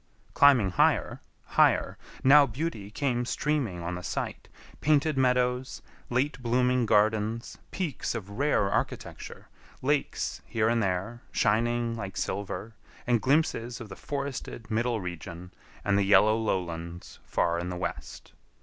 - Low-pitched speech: Yes, low, 115 Hz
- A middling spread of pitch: Yes, average, 4.5 semitones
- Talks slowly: Yes, slow, 130 wpm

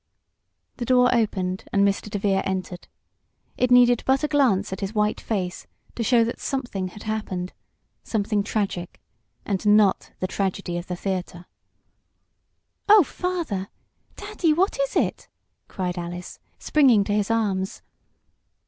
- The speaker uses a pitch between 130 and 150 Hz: No, high, 205 Hz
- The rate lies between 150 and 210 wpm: No, average, 140 wpm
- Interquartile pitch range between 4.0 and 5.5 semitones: Yes, average, 4.5 semitones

